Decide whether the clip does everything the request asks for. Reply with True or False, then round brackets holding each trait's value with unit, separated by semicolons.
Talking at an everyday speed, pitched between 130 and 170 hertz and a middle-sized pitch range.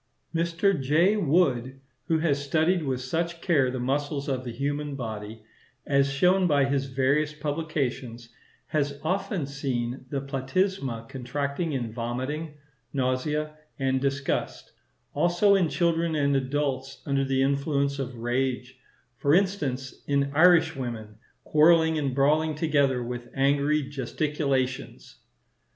False (120 wpm; 140 Hz; 3.0 semitones)